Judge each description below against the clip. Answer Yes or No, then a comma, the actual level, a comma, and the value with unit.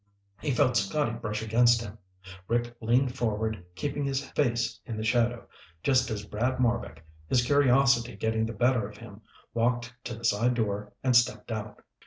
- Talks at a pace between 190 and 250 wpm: No, average, 170 wpm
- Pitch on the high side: No, low, 115 Hz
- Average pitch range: No, narrow, 2.1 semitones